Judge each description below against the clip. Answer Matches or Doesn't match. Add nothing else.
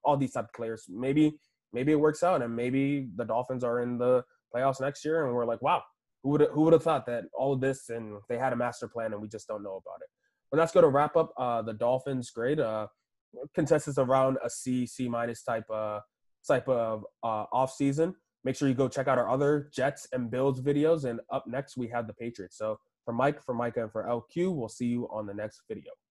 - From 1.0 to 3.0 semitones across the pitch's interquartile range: Doesn't match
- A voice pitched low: Matches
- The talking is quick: Matches